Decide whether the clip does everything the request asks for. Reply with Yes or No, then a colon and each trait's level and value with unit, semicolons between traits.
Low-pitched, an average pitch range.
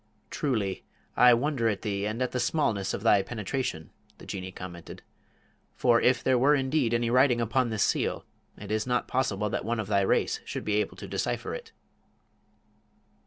Yes: low, 115 Hz; average, 3.9 semitones